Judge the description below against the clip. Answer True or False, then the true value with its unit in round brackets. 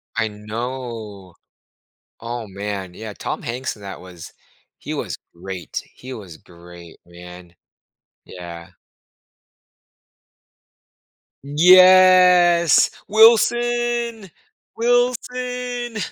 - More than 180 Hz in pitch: False (120 Hz)